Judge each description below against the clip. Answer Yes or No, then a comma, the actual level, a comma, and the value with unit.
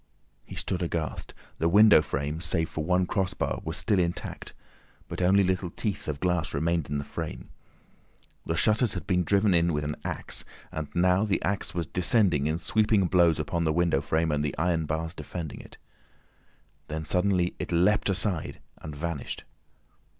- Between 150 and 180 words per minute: Yes, average, 170 wpm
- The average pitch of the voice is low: Yes, very low, 85 Hz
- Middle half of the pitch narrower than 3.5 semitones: Yes, average, 2.9 semitones